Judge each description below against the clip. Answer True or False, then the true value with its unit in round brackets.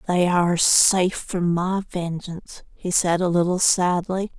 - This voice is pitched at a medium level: True (180 Hz)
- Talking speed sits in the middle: True (150 wpm)